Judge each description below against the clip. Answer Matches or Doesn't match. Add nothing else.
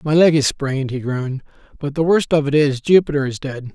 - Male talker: Matches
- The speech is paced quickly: Matches